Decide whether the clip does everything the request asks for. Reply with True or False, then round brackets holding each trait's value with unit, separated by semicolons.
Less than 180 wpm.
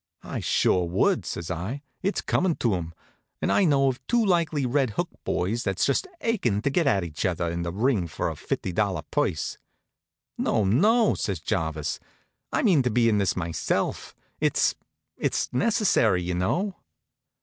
True (170 wpm)